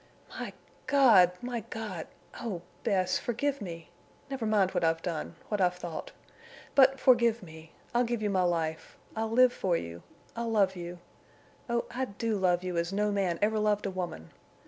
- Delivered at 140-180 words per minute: Yes, average, 170 wpm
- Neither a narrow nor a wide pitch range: Yes, average, 4.7 semitones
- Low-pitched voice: No, high, 200 Hz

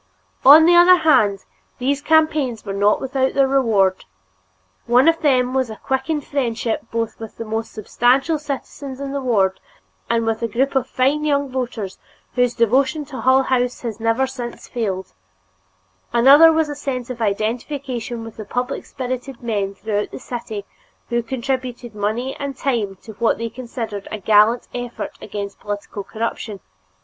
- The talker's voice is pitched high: Yes, high, 245 Hz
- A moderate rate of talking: Yes, average, 160 wpm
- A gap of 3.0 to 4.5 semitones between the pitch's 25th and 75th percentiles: Yes, average, 3.4 semitones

